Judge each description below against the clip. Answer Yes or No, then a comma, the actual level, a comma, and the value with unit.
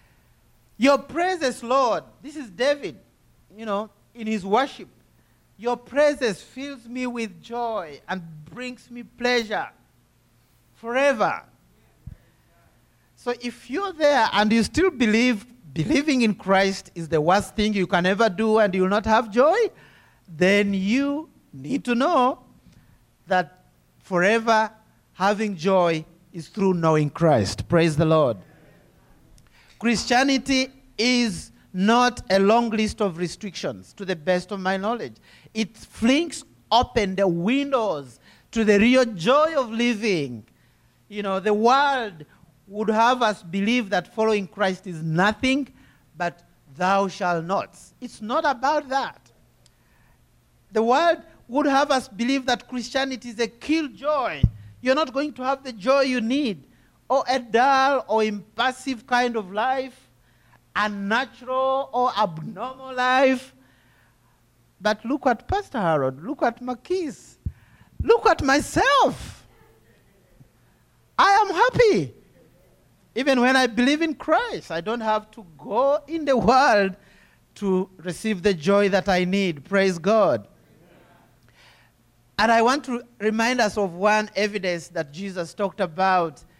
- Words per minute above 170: No, slow, 135 wpm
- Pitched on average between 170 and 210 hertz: No, high, 225 Hz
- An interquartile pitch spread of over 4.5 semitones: Yes, wide, 5.4 semitones